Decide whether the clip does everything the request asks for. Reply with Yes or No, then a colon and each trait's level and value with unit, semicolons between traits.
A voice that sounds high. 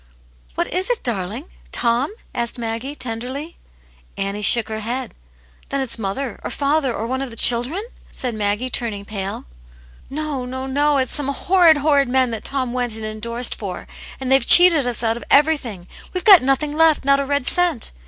Yes: very high, 255 Hz